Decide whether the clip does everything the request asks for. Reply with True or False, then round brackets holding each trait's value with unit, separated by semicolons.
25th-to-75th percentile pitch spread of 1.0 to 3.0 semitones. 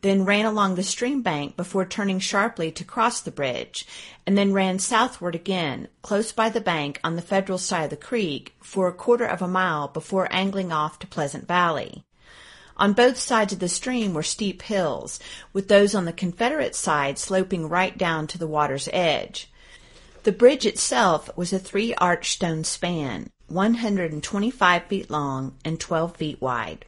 False (3.8 semitones)